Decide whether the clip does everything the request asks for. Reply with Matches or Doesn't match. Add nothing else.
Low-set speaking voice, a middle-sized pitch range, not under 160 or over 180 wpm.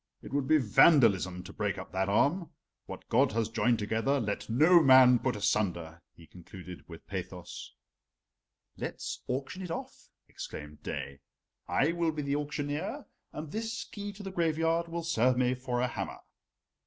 Doesn't match